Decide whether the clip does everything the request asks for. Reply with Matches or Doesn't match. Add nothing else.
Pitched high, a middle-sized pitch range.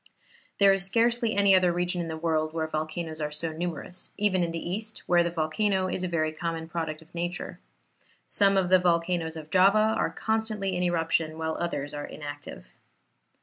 Doesn't match